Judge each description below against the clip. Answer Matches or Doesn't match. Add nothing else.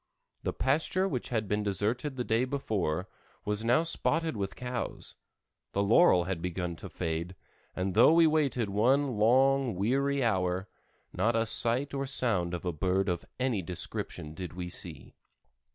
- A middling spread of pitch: Doesn't match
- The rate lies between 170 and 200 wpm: Doesn't match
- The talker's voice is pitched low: Matches